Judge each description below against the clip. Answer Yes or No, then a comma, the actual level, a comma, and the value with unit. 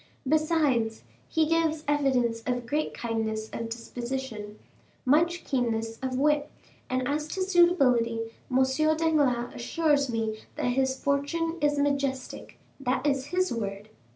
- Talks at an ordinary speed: No, slow, 125 wpm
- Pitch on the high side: Yes, very high, 265 Hz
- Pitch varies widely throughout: No, average, 4.5 semitones